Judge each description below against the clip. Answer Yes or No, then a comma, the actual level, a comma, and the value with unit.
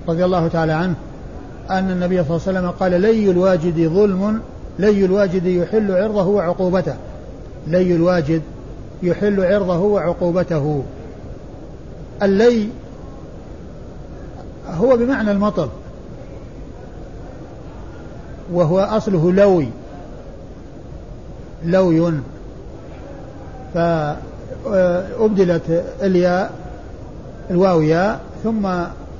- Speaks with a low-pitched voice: No, medium, 180 Hz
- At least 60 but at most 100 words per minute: Yes, average, 75 wpm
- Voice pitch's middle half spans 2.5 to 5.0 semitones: Yes, average, 2.8 semitones